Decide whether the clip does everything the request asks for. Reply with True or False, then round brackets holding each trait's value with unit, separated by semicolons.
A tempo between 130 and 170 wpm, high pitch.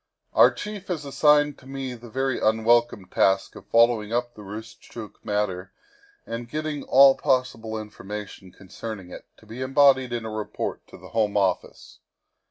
False (165 wpm; 115 Hz)